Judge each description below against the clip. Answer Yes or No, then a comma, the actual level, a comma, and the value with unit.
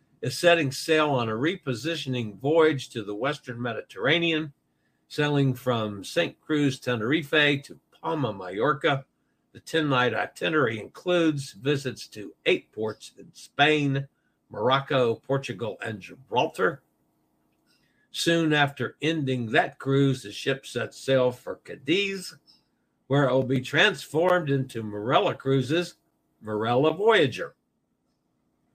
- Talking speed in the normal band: No, slow, 115 wpm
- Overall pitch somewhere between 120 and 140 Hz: Yes, low, 135 Hz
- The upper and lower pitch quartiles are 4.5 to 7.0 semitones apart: No, average, 4.0 semitones